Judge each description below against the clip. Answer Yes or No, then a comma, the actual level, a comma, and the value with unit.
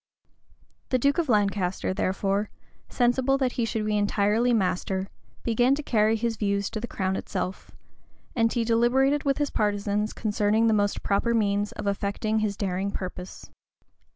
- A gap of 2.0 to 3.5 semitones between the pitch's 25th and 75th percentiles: Yes, average, 2.9 semitones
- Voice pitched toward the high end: Yes, high, 215 Hz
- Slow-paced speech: No, average, 155 wpm